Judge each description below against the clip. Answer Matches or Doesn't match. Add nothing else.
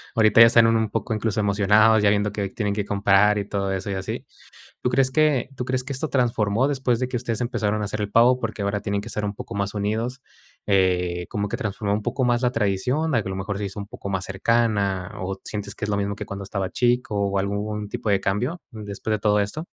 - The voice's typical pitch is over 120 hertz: Doesn't match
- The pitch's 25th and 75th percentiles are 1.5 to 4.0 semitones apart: Matches